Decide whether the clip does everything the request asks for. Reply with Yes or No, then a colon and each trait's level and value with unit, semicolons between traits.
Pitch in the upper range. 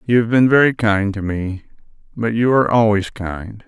No: low, 110 Hz